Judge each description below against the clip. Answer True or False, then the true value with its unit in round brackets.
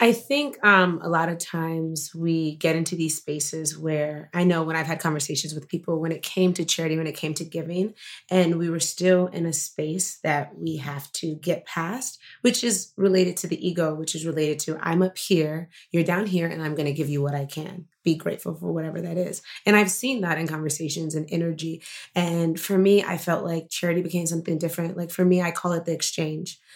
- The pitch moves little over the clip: True (2.0 semitones)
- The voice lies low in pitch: False (165 Hz)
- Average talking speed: False (225 wpm)